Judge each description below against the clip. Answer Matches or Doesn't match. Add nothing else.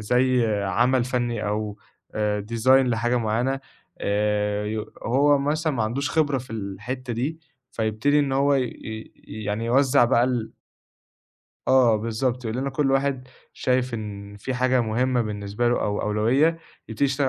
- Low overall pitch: Matches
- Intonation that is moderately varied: Matches